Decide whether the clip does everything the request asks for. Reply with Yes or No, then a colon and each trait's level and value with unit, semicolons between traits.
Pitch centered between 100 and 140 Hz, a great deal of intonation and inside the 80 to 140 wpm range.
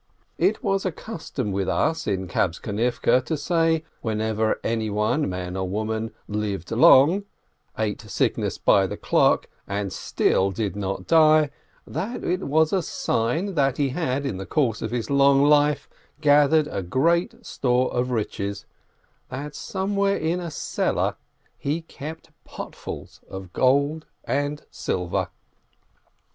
Yes: low, 135 Hz; wide, 6.8 semitones; slow, 135 wpm